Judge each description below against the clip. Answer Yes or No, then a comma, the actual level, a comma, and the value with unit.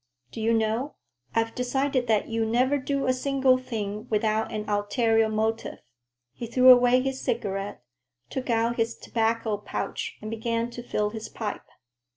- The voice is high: Yes, high, 230 Hz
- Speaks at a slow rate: No, average, 160 wpm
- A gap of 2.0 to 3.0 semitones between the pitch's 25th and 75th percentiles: Yes, narrow, 2.5 semitones